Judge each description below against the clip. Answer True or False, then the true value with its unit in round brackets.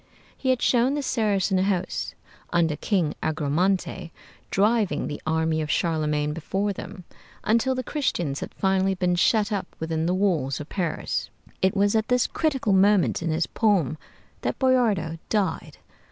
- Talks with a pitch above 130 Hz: True (190 Hz)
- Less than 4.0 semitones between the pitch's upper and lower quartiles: False (4.9 semitones)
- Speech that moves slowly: False (155 wpm)